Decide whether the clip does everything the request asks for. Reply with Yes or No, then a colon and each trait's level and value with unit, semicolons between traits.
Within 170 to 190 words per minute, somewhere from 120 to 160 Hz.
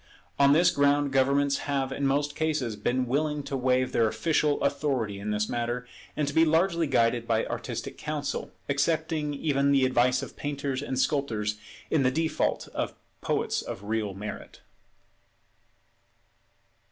No: average, 150 wpm; medium, 140 Hz